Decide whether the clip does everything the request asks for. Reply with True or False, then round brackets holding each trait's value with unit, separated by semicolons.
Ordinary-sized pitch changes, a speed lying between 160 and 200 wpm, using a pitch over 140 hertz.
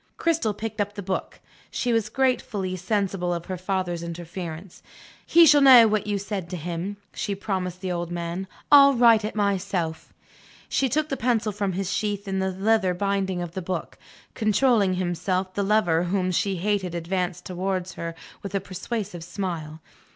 True (3.0 semitones; 175 wpm; 190 Hz)